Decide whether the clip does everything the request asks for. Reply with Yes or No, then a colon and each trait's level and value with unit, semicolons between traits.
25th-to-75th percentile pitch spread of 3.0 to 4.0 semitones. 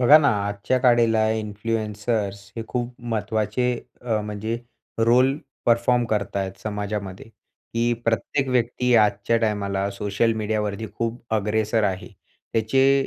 No: narrow, 2.5 semitones